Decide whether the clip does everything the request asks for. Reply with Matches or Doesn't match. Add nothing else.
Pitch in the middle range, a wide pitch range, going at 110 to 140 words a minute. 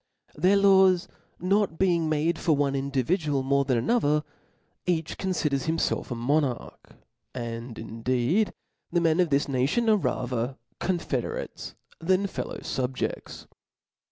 Matches